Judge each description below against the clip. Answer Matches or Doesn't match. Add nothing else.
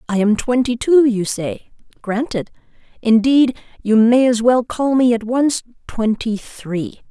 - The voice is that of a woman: Matches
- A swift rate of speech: Doesn't match